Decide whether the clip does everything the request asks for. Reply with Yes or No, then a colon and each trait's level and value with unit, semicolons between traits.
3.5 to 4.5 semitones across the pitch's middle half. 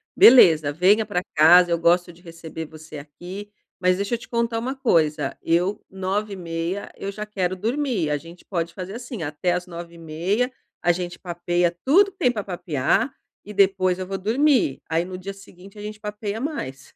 Yes: average, 3.8 semitones